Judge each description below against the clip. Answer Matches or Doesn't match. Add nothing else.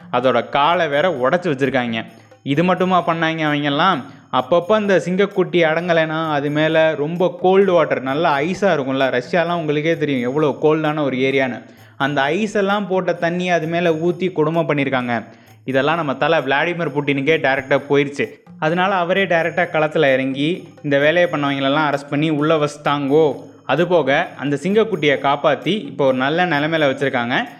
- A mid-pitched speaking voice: Matches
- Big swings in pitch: Doesn't match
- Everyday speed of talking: Doesn't match